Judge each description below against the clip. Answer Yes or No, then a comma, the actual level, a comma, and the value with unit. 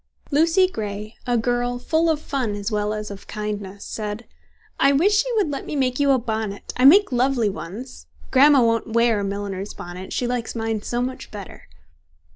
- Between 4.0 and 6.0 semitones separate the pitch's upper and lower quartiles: Yes, average, 4.7 semitones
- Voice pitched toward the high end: Yes, high, 235 Hz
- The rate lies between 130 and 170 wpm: No, average, 190 wpm